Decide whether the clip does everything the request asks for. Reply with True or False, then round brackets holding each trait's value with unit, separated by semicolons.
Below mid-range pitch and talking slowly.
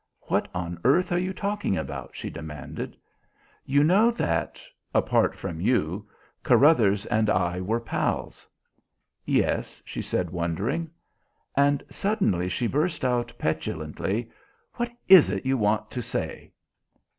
True (115 Hz; 130 wpm)